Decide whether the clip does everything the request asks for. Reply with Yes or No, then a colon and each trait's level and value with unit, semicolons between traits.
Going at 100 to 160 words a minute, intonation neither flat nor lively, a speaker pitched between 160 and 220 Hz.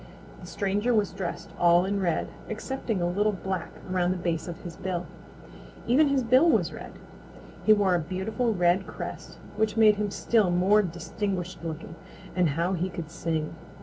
No: average, 175 wpm; average, 3.4 semitones; high, 190 Hz